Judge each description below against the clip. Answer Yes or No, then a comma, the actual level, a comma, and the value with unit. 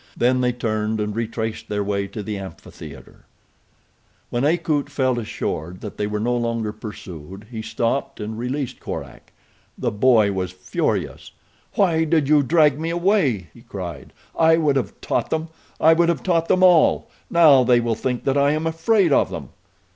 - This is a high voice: No, low, 125 Hz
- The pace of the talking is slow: No, average, 175 wpm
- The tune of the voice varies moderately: No, wide, 6.8 semitones